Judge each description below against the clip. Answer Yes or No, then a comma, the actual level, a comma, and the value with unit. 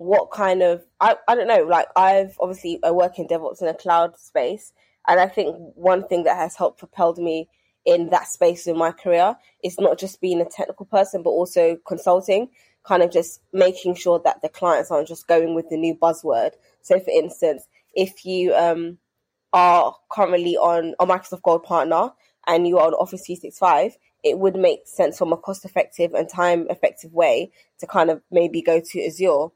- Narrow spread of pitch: Yes, narrow, 2.1 semitones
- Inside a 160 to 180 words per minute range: No, average, 195 wpm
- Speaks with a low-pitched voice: No, medium, 180 Hz